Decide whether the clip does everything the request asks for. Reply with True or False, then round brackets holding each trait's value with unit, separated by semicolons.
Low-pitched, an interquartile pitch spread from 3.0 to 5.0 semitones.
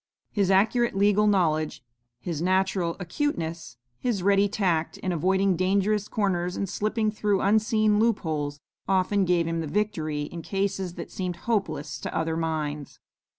False (190 Hz; 3.8 semitones)